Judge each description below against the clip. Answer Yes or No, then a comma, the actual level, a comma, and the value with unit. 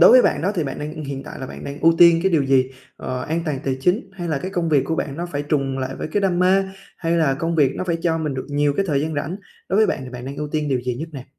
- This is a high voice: No, medium, 150 Hz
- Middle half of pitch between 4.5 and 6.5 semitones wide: No, average, 3.8 semitones